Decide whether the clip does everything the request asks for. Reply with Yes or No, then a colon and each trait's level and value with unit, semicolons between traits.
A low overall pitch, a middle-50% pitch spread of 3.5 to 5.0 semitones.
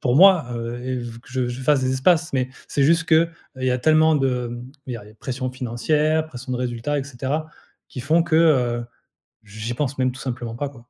Yes: low, 130 Hz; average, 4.0 semitones